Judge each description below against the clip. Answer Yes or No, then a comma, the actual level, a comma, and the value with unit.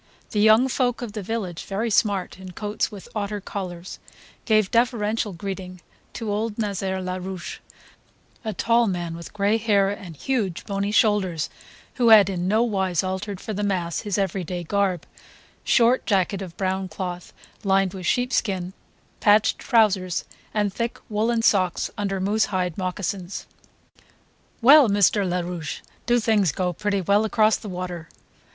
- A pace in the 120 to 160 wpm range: Yes, average, 150 wpm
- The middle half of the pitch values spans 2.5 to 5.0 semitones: Yes, average, 2.8 semitones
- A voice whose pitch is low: No, high, 200 Hz